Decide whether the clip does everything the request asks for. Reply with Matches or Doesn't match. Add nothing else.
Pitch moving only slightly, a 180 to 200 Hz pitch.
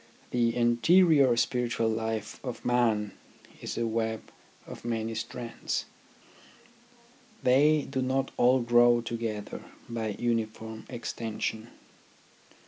Doesn't match